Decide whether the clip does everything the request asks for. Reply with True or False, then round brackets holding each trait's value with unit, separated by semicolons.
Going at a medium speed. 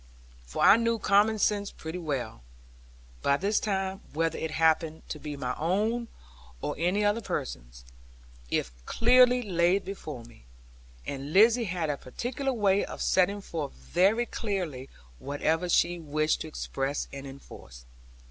True (145 wpm)